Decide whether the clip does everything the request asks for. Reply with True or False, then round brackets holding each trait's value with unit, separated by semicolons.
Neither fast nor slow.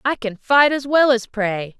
False (235 wpm)